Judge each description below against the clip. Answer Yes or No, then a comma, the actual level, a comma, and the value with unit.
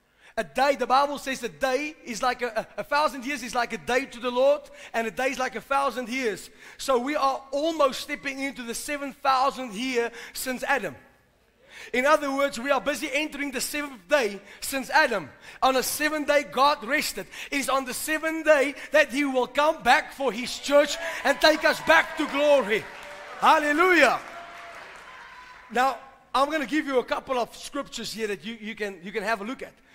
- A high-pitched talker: Yes, very high, 270 Hz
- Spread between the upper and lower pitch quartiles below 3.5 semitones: Yes, average, 2.8 semitones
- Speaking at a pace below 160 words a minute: No, average, 200 wpm